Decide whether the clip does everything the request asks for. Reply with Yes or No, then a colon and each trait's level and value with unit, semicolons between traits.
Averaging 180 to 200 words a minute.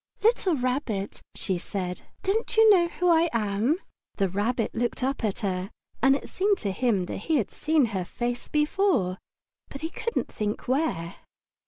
No: average, 170 wpm